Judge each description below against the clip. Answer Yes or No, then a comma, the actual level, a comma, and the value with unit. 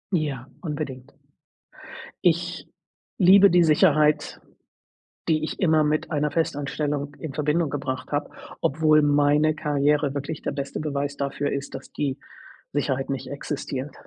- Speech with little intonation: Yes, narrow, 1.7 semitones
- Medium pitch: Yes, medium, 145 Hz